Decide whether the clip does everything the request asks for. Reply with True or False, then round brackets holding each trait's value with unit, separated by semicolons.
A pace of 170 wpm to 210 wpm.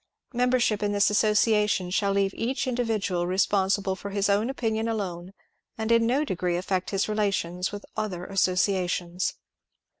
False (150 wpm)